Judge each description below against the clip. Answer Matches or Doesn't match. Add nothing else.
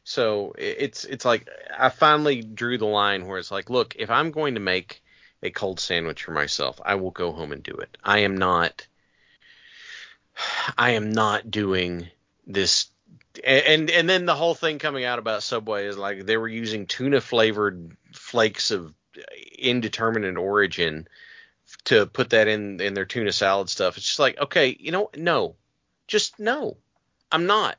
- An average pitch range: Doesn't match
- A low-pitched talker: Matches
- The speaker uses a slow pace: Doesn't match